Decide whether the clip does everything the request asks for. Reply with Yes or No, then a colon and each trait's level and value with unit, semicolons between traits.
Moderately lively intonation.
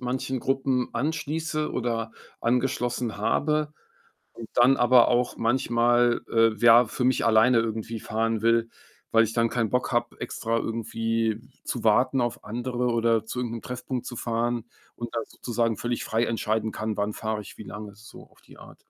No: narrow, 1.7 semitones